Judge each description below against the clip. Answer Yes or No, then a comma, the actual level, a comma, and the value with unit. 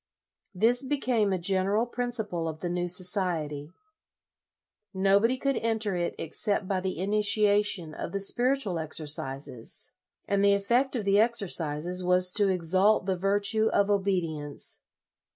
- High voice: Yes, high, 195 Hz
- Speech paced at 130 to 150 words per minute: Yes, average, 140 wpm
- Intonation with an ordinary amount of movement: Yes, average, 3.3 semitones